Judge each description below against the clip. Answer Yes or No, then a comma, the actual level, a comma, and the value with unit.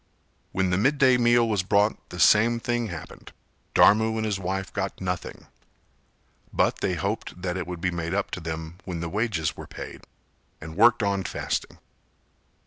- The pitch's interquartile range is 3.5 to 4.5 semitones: Yes, average, 3.9 semitones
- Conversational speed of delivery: Yes, average, 170 wpm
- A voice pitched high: No, very low, 95 Hz